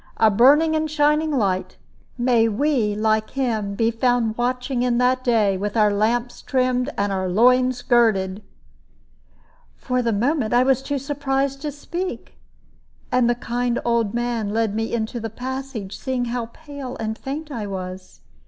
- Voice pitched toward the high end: Yes, high, 240 Hz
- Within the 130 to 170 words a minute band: Yes, average, 160 wpm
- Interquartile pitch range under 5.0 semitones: Yes, average, 3.4 semitones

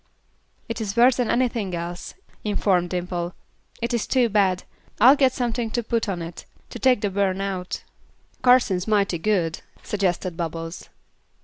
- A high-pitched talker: Yes, high, 200 Hz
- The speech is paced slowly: No, average, 150 wpm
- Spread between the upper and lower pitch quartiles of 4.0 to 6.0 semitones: Yes, average, 4.7 semitones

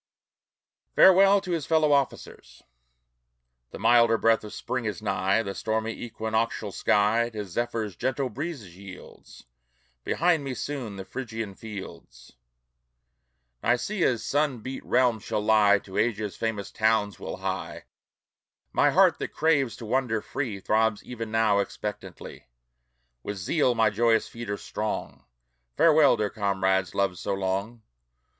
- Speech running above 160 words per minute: No, slow, 135 wpm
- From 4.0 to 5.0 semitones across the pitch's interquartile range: No, average, 3.6 semitones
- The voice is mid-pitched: No, low, 110 Hz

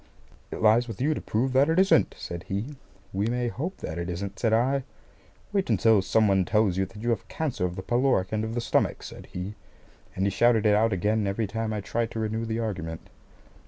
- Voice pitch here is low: Yes, low, 110 Hz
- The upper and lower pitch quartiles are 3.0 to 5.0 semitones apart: Yes, average, 3.4 semitones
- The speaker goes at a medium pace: No, fast, 230 wpm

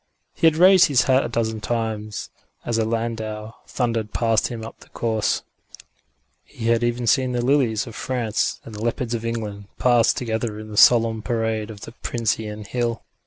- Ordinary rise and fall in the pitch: No, narrow, 1.7 semitones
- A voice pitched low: Yes, low, 115 Hz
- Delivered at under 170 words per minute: No, average, 180 wpm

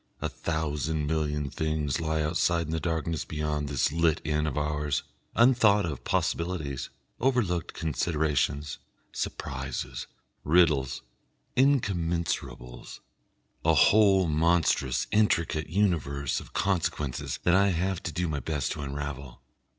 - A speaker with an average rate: No, slow, 120 wpm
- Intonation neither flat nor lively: Yes, average, 3.0 semitones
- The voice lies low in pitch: Yes, very low, 80 Hz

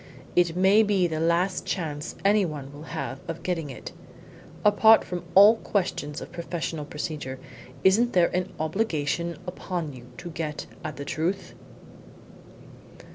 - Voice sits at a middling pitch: Yes, medium, 170 Hz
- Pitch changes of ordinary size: Yes, average, 3.7 semitones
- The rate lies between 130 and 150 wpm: Yes, slow, 135 wpm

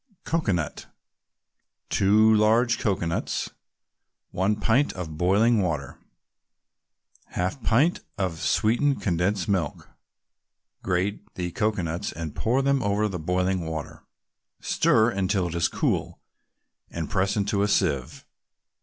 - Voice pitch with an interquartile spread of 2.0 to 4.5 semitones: Yes, average, 3.9 semitones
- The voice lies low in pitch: Yes, very low, 95 Hz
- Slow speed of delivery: Yes, slow, 115 wpm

